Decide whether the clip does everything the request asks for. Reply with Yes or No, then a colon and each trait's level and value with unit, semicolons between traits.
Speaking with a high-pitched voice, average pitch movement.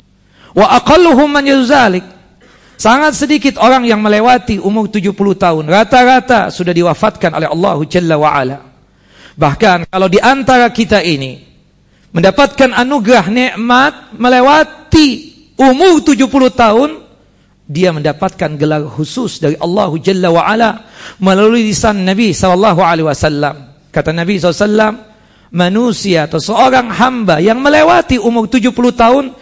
No: high, 215 Hz; wide, 6.2 semitones